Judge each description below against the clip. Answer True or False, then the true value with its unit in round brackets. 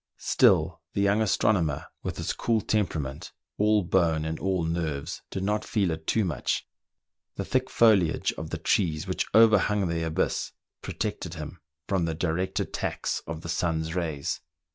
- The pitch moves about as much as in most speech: True (4.3 semitones)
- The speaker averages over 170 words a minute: False (160 wpm)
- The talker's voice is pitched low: True (85 Hz)